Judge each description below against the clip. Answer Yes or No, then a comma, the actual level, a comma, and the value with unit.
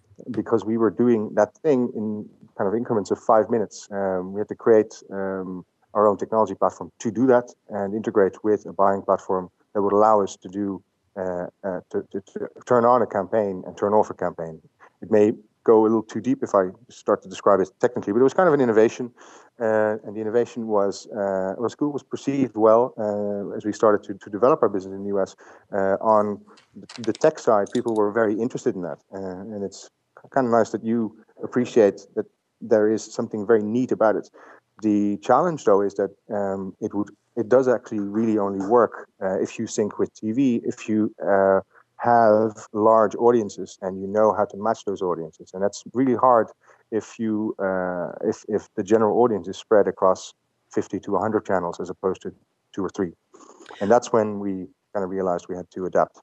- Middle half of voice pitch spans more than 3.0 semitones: No, narrow, 2.5 semitones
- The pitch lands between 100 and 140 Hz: Yes, low, 105 Hz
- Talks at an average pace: No, fast, 210 wpm